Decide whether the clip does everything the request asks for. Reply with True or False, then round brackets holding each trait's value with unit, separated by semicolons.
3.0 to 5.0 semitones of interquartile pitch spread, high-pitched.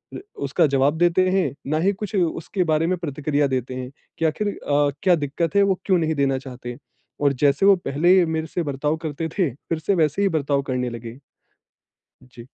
False (4.2 semitones; 155 Hz)